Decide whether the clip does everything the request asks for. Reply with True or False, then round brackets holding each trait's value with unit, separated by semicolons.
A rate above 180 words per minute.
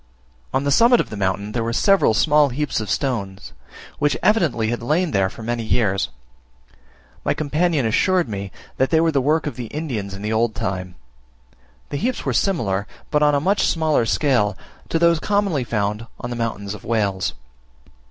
True (190 wpm)